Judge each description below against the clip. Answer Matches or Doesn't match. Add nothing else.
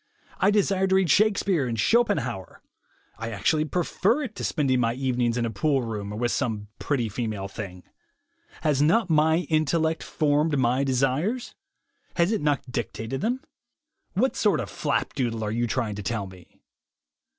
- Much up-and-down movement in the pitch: Matches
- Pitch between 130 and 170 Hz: Matches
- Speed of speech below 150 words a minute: Doesn't match